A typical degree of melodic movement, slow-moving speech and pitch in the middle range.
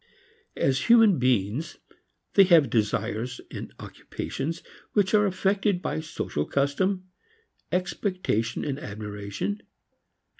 No: wide, 9.0 semitones; slow, 100 wpm; medium, 155 Hz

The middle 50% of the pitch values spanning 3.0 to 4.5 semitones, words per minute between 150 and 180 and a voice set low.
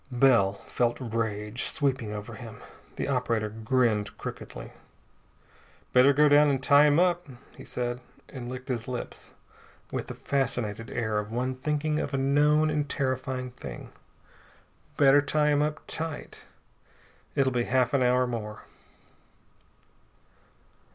No: average, 3.7 semitones; slow, 135 wpm; low, 130 Hz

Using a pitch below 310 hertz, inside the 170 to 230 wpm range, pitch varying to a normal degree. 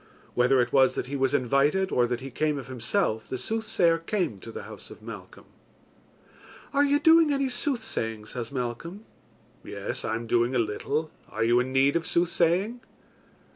No: medium, 140 Hz; average, 175 wpm; wide, 7.8 semitones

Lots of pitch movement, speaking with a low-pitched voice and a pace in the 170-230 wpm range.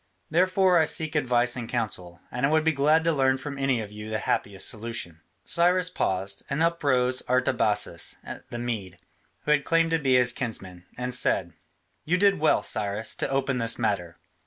Yes: wide, 6.4 semitones; low, 125 Hz; average, 190 wpm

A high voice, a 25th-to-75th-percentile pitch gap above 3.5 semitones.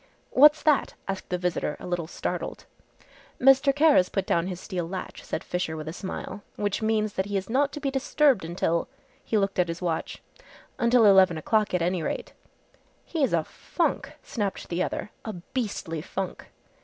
Yes: high, 195 Hz; average, 5.0 semitones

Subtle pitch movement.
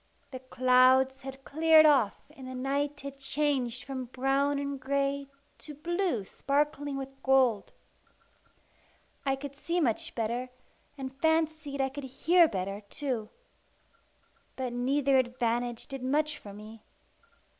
Yes: narrow, 2.2 semitones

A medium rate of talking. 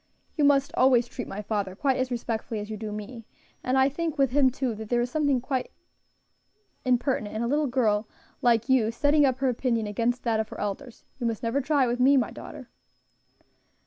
No: fast, 210 wpm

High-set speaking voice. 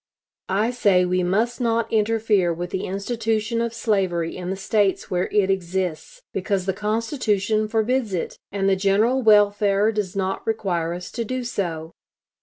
Yes: high, 205 Hz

